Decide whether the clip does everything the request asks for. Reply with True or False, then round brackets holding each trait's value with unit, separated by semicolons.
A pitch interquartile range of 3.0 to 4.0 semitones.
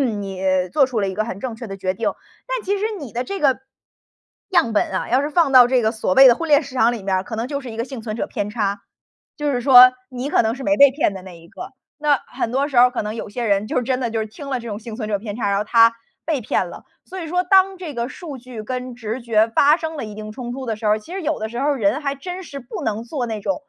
False (4.6 semitones)